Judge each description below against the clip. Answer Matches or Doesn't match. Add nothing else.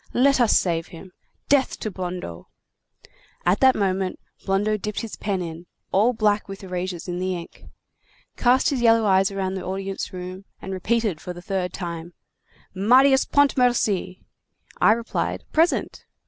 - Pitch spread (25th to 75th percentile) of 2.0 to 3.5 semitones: Doesn't match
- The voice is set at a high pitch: Matches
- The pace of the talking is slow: Doesn't match